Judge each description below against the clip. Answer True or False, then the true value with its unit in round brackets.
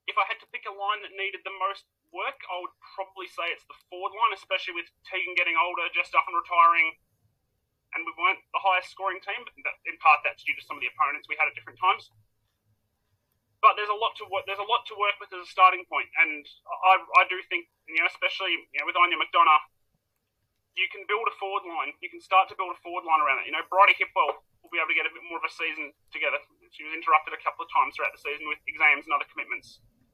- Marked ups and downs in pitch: False (4.4 semitones)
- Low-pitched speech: False (180 Hz)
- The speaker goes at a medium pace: False (255 wpm)